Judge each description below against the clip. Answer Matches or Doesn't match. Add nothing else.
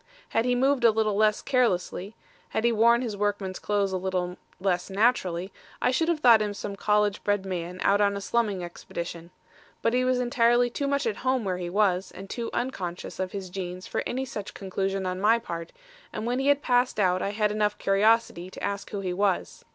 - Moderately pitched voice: Doesn't match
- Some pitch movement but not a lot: Matches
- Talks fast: Matches